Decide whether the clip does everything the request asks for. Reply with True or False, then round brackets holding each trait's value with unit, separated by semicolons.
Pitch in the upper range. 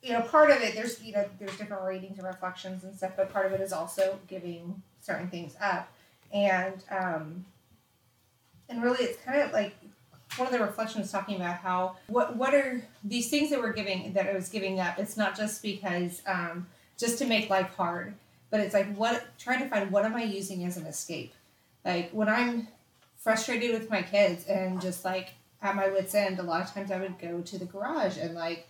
True (195 Hz)